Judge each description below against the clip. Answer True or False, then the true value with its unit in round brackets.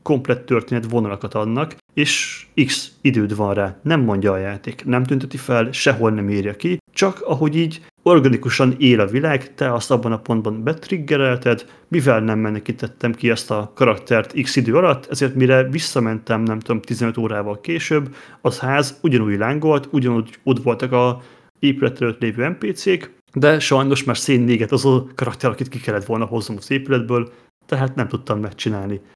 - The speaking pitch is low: True (125 Hz)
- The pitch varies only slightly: False (3.6 semitones)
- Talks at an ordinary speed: False (165 wpm)